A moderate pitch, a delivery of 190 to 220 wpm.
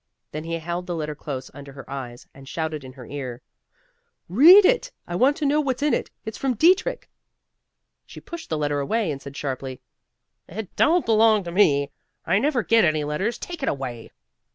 Yes: medium, 170 Hz; average, 195 wpm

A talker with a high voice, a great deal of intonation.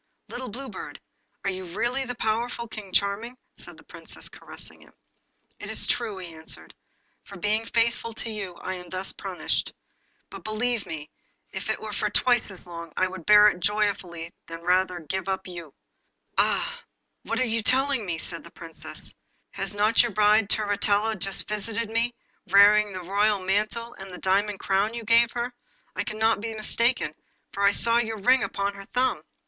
No: high, 210 Hz; average, 3.3 semitones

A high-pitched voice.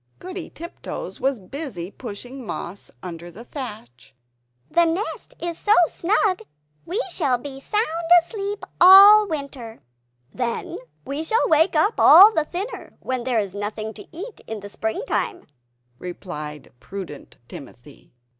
Yes: very high, 275 Hz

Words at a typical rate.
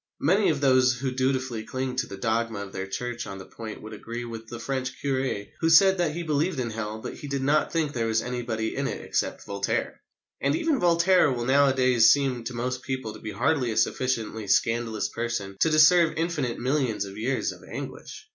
No: fast, 210 wpm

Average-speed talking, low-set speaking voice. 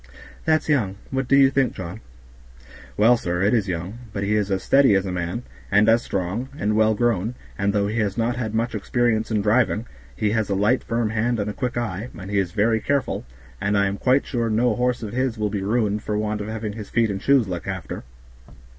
No: fast, 235 wpm; low, 110 Hz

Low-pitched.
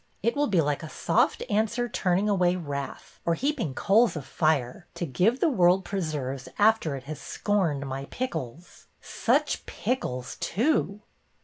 No: medium, 175 Hz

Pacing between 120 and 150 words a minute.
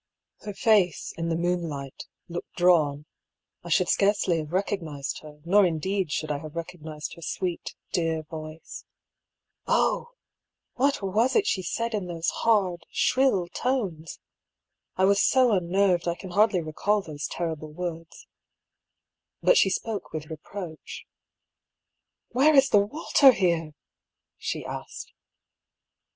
Yes: average, 140 wpm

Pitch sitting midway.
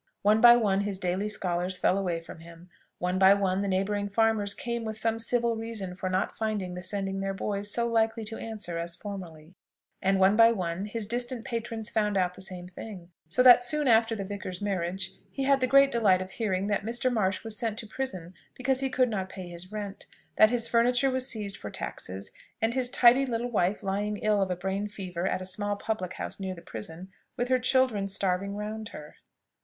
No: high, 205 Hz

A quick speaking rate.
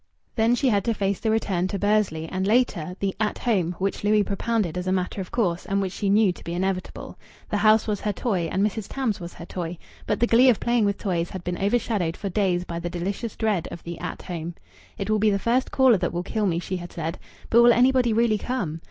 Yes: fast, 250 wpm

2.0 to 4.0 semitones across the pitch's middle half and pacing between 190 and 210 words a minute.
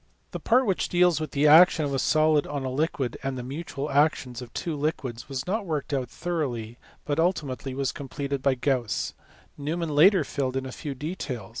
Yes: average, 3.4 semitones; average, 195 wpm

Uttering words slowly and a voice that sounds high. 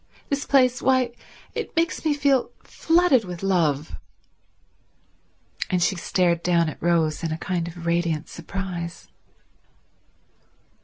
No: slow, 115 wpm; medium, 180 Hz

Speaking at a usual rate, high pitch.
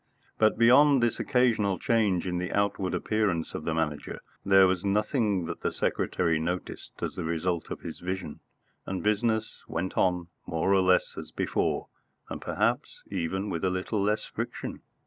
No: average, 165 wpm; very low, 95 Hz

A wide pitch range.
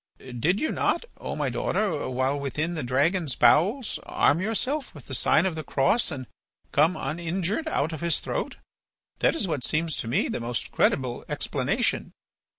Yes: wide, 5.7 semitones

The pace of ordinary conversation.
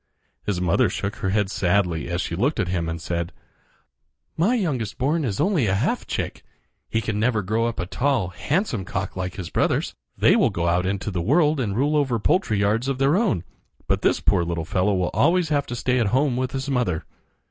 No: fast, 215 wpm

